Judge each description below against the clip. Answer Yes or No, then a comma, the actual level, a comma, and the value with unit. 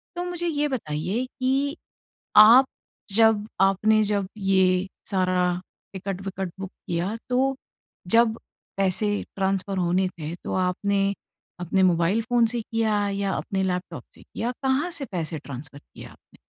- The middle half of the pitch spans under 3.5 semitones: No, average, 3.8 semitones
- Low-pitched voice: No, high, 195 Hz